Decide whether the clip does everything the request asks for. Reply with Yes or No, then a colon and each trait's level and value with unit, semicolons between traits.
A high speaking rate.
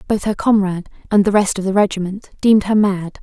Yes: fast, 225 wpm